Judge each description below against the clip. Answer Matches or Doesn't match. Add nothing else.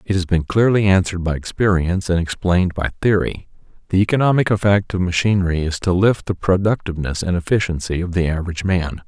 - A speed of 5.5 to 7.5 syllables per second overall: Matches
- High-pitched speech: Doesn't match